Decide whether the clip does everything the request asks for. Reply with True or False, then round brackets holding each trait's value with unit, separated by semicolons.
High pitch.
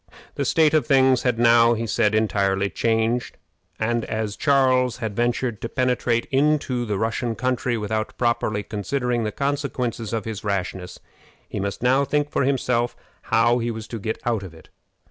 False (115 Hz)